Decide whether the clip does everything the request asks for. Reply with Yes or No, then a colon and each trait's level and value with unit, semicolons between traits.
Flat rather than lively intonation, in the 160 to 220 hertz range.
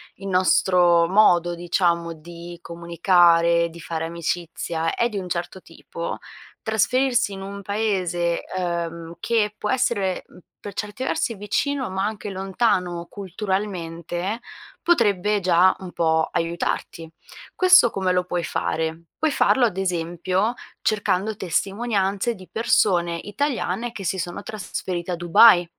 No: average, 3.4 semitones; medium, 185 Hz